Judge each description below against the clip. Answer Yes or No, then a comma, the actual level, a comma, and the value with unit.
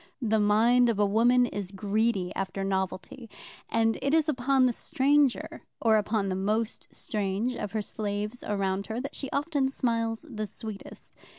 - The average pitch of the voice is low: No, high, 220 Hz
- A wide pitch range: No, average, 3.5 semitones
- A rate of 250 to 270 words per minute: No, average, 165 wpm